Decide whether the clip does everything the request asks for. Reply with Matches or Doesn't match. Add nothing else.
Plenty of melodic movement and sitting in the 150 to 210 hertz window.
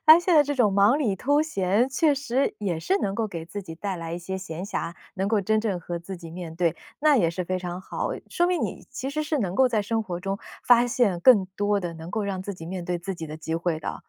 Matches